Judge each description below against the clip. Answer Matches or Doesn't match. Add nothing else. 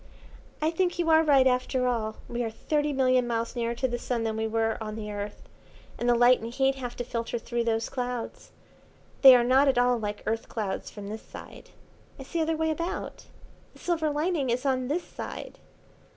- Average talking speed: Doesn't match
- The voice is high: Matches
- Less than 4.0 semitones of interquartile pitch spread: Matches